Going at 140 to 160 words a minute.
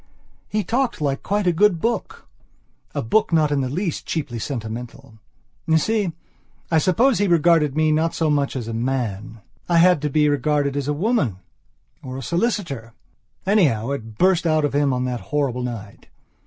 No: average, 175 wpm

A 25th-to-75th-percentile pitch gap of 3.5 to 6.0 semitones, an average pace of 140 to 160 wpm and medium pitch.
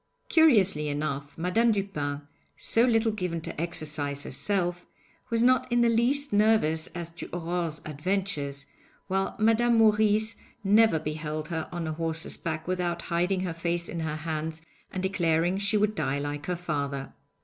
Yes: average, 5.1 semitones; average, 155 wpm; medium, 175 Hz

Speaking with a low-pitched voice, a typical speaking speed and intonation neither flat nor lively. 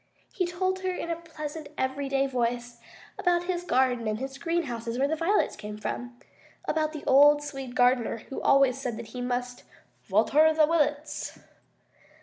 No: very high, 275 Hz; average, 160 wpm; average, 4.4 semitones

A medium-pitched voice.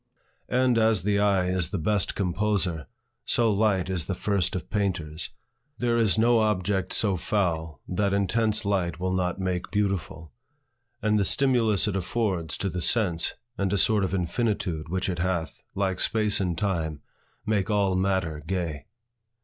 No: very low, 95 Hz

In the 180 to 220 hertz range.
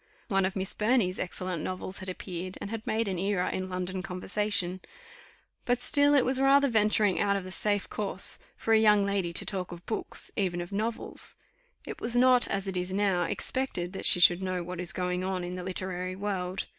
Yes: high, 190 Hz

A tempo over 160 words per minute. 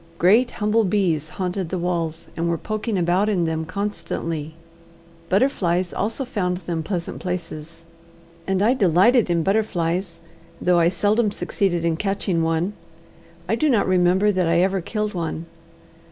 No: average, 150 wpm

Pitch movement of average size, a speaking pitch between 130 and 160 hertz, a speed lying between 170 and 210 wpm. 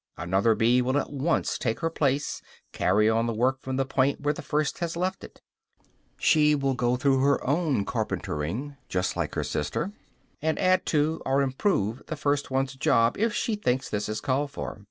Yes: average, 3.9 semitones; low, 135 Hz; average, 195 wpm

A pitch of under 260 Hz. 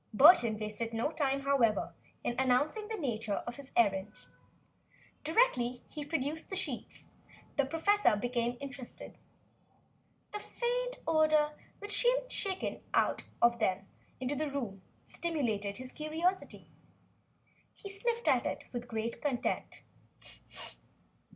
No: very high, 275 Hz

